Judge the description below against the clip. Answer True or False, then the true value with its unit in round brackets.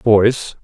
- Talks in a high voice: False (110 Hz)